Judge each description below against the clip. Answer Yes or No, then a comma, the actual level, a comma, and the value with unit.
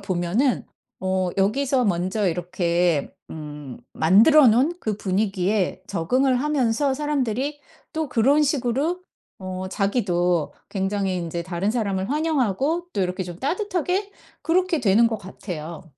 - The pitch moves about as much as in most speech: No, wide, 7.3 semitones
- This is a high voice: Yes, high, 210 Hz